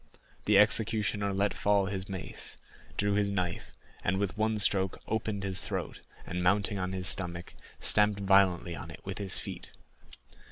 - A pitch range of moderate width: No, narrow, 1.7 semitones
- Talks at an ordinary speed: Yes, average, 160 wpm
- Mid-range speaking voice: No, low, 100 Hz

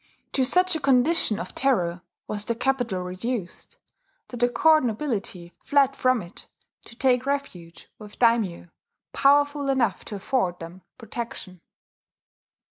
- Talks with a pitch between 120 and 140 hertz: No, high, 240 Hz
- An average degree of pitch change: No, wide, 6.2 semitones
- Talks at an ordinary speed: No, slow, 130 wpm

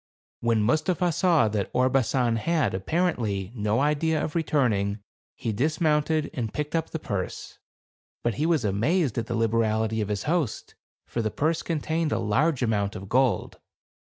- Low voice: Yes, low, 125 Hz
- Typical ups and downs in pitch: No, wide, 6.4 semitones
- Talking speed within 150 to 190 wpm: Yes, average, 160 wpm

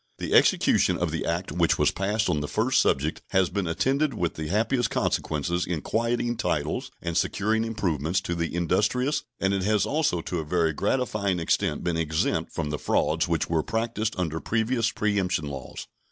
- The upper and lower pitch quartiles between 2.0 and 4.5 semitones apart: No, average, 5.2 semitones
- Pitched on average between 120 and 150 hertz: No, very low, 95 Hz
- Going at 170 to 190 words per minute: Yes, average, 180 wpm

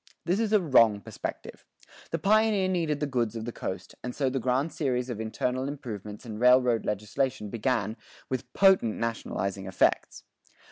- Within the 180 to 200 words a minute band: No, average, 160 wpm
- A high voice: No, low, 125 Hz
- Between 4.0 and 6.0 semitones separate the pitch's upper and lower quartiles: Yes, average, 5.1 semitones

